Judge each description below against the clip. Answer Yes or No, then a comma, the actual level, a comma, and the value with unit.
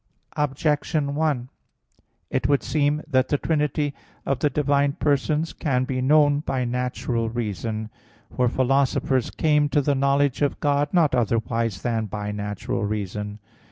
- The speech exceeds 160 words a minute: No, average, 140 wpm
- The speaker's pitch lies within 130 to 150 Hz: Yes, low, 135 Hz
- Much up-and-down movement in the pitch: No, average, 3.9 semitones